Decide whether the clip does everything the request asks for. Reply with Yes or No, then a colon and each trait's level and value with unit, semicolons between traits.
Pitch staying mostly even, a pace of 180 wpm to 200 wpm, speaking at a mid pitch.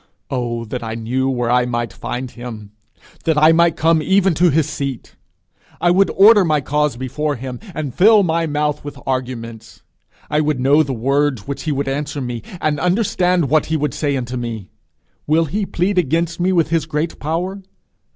No: average, 4.6 semitones; average, 190 wpm; medium, 150 Hz